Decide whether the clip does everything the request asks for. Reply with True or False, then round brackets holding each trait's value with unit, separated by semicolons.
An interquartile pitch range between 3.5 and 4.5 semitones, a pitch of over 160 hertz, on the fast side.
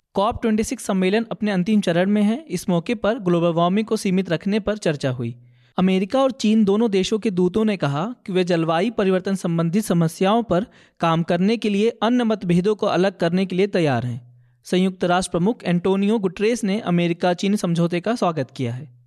True (3.8 semitones; 190 Hz; 195 wpm)